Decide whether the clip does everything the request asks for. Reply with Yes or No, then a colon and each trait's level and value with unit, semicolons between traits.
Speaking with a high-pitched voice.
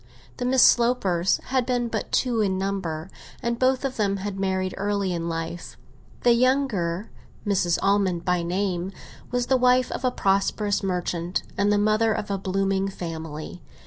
Yes: high, 195 Hz